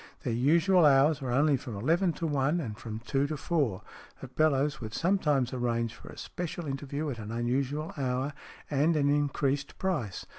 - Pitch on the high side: No, medium, 140 Hz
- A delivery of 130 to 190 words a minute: Yes, average, 180 wpm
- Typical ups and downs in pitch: Yes, average, 3.7 semitones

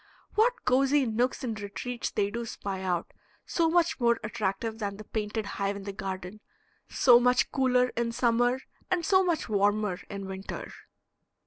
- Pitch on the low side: No, high, 230 Hz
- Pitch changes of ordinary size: Yes, average, 4.0 semitones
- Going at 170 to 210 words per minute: No, average, 160 wpm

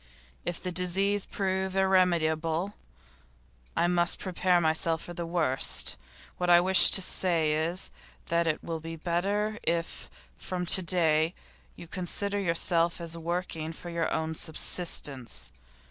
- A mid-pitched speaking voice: Yes, medium, 170 Hz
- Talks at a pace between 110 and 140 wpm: Yes, slow, 135 wpm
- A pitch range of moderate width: No, narrow, 2.1 semitones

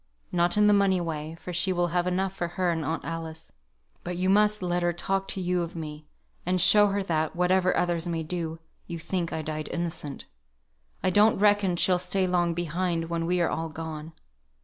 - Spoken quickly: Yes, fast, 210 wpm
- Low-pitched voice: No, medium, 175 Hz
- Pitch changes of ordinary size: No, narrow, 2.1 semitones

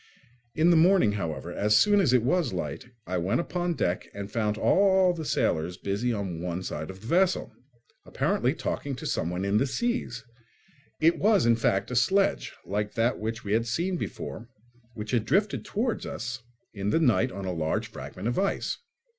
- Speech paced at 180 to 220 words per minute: Yes, average, 185 wpm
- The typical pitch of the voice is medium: No, low, 115 Hz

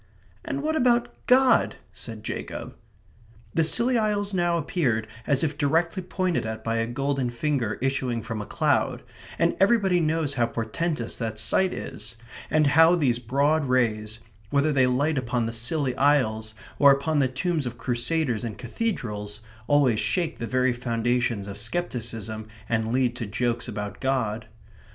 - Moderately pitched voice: No, low, 130 Hz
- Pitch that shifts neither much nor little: No, wide, 5.9 semitones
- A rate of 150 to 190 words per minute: Yes, average, 155 wpm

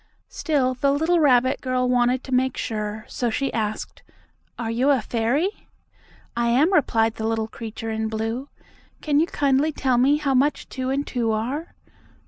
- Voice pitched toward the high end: Yes, very high, 255 Hz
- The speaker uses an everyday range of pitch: Yes, average, 3.8 semitones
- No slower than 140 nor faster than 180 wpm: Yes, average, 170 wpm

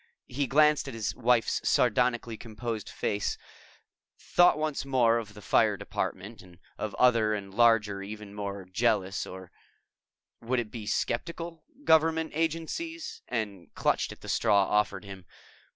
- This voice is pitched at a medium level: No, low, 115 Hz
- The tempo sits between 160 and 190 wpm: No, average, 145 wpm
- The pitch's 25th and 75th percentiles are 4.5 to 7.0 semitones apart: Yes, average, 4.9 semitones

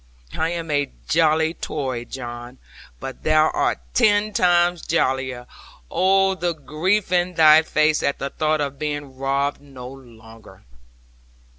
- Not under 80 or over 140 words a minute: Yes, slow, 135 wpm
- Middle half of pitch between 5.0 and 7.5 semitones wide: No, average, 4.2 semitones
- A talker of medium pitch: Yes, medium, 155 Hz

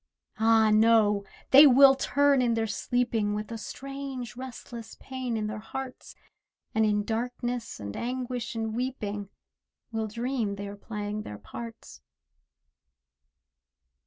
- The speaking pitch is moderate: No, high, 230 Hz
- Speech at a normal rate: No, slow, 130 wpm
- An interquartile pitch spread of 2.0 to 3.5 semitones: Yes, average, 2.9 semitones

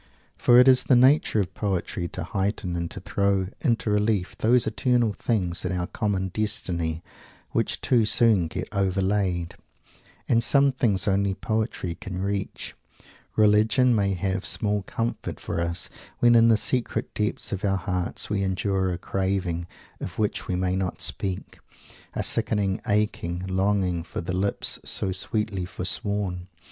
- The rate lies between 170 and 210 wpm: No, average, 155 wpm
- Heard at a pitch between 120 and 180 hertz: No, low, 100 Hz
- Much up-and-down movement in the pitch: No, average, 2.8 semitones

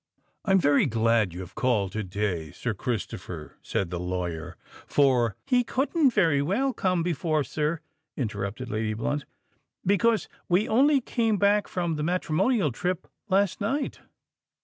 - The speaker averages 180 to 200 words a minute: No, average, 150 wpm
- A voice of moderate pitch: Yes, medium, 150 Hz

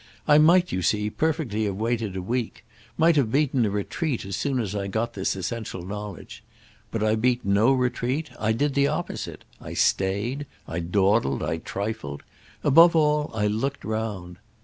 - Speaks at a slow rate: No, average, 170 wpm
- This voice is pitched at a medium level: No, low, 110 Hz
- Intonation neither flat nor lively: No, wide, 5.7 semitones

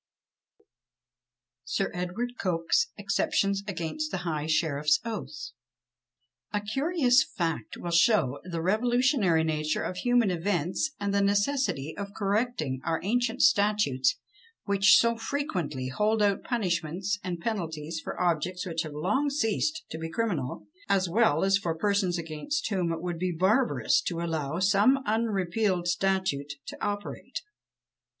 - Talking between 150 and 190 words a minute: No, slow, 135 wpm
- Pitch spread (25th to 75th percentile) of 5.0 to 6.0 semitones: Yes, average, 5.3 semitones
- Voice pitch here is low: No, high, 190 Hz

